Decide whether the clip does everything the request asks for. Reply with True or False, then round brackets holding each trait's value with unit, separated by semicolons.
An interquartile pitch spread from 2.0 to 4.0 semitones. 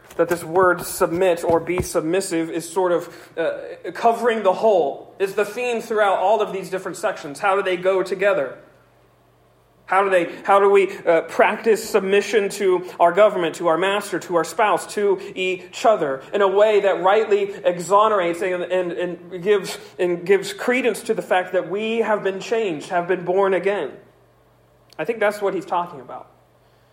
True (2.7 semitones)